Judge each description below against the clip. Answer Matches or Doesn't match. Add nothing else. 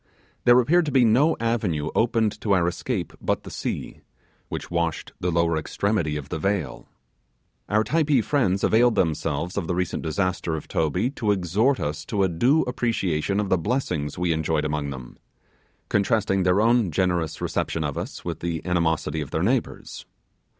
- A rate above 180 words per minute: Doesn't match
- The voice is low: Matches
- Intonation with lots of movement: Matches